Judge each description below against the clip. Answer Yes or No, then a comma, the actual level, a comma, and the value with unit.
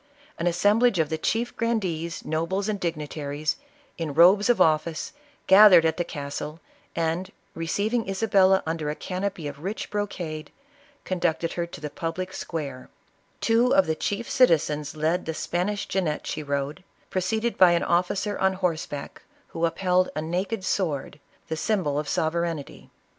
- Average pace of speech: Yes, average, 160 wpm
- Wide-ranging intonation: No, average, 3.7 semitones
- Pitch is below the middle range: No, medium, 170 Hz